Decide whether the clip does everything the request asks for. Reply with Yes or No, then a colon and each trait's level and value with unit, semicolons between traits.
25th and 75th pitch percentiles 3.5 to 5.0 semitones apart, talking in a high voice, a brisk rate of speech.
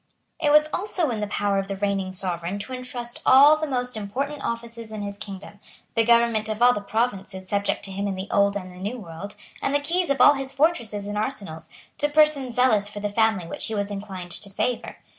Yes: average, 4.1 semitones; high, 215 Hz; fast, 230 wpm